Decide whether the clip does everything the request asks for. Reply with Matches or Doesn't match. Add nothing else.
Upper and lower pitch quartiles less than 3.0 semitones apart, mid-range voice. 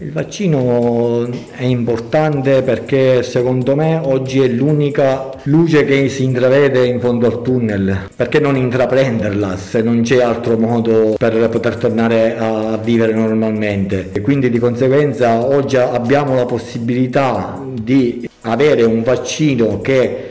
Doesn't match